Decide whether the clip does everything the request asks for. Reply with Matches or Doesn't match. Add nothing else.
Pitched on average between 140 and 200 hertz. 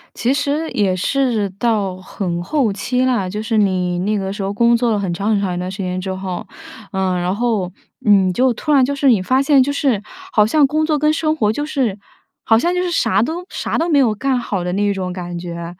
Doesn't match